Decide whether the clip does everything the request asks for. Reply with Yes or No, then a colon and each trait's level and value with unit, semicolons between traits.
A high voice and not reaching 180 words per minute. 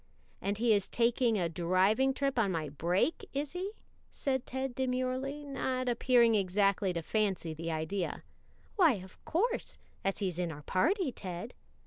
Yes: high, 220 Hz; average, 160 wpm